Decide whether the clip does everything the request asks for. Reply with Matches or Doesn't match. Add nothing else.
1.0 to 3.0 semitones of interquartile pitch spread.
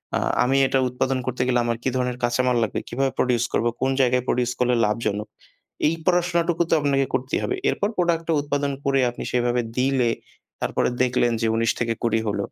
Matches